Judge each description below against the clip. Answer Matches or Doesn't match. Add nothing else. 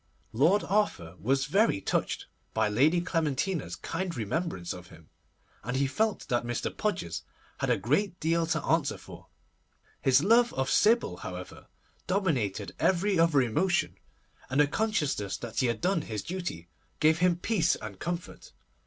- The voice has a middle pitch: Matches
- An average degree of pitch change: Doesn't match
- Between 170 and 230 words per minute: Doesn't match